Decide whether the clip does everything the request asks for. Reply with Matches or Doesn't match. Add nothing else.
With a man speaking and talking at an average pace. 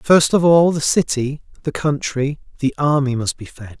Matches